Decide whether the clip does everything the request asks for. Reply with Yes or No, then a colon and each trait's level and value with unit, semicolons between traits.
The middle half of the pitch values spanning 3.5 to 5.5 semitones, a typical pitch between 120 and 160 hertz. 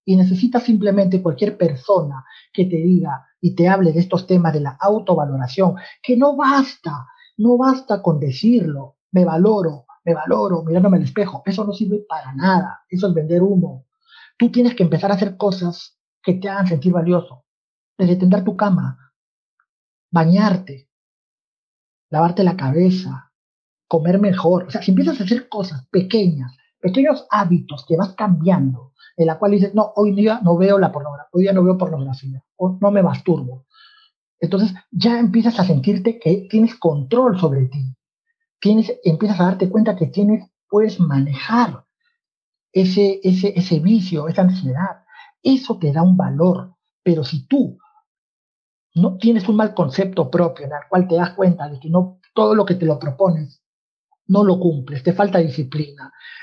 No: average, 4.1 semitones; medium, 185 Hz